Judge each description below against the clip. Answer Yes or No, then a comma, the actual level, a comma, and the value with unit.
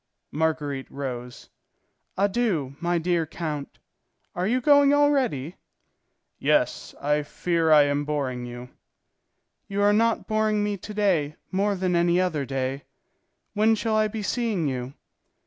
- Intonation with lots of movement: Yes, wide, 6.5 semitones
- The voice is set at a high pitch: No, medium, 175 Hz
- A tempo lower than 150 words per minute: Yes, slow, 135 wpm